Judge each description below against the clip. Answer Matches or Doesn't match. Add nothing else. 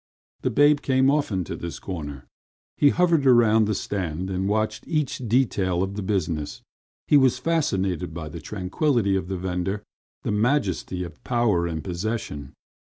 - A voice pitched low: Matches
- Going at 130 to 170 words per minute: Matches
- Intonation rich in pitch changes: Matches